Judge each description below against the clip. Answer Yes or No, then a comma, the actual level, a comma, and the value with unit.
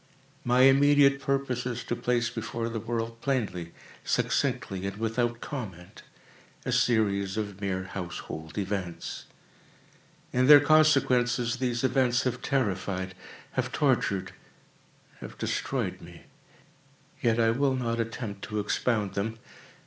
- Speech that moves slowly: Yes, slow, 115 wpm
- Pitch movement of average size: Yes, average, 4.2 semitones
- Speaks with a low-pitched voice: Yes, low, 115 Hz